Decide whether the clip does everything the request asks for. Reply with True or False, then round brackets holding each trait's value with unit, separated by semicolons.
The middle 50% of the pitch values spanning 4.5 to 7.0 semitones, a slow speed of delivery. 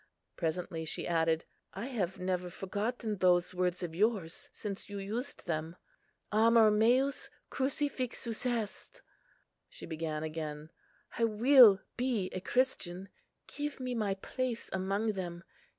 True (5.2 semitones; 130 wpm)